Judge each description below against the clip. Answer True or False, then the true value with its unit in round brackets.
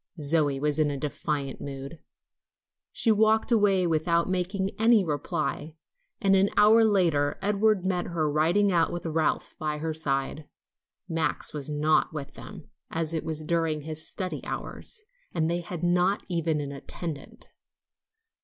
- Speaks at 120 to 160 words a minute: True (150 wpm)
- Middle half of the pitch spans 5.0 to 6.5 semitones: False (3.8 semitones)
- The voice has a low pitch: False (165 Hz)